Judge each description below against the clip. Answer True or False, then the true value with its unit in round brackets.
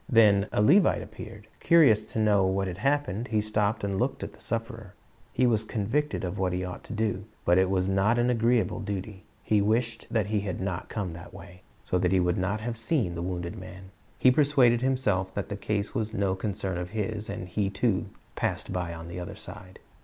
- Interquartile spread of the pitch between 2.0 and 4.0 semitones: True (3.3 semitones)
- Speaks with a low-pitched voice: True (100 Hz)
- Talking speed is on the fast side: True (220 wpm)